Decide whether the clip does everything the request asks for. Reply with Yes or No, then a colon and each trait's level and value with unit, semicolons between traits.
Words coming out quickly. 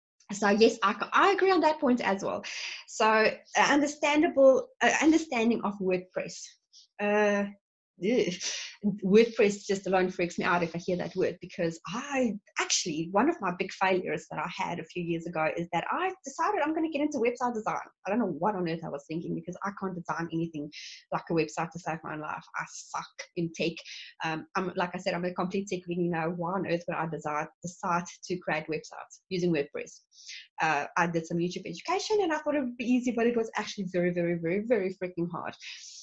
Yes: fast, 215 wpm